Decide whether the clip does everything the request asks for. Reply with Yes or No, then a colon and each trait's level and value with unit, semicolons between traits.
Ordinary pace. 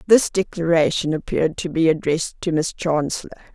Yes: average, 150 wpm